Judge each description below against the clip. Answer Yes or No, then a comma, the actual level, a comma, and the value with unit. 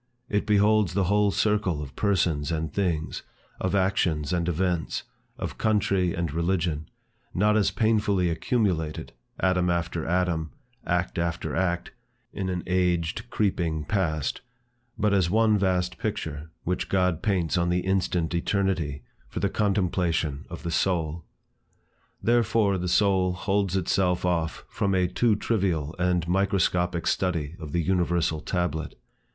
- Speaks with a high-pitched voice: No, very low, 90 Hz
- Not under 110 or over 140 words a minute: Yes, slow, 135 wpm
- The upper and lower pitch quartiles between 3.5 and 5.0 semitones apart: No, average, 2.7 semitones